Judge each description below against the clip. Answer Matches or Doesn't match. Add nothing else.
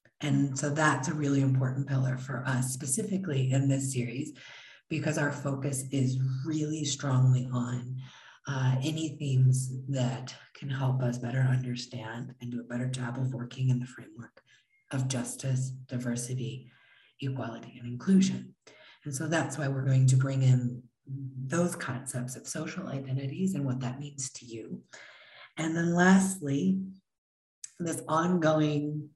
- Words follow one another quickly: Doesn't match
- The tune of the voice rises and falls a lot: Doesn't match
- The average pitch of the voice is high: Doesn't match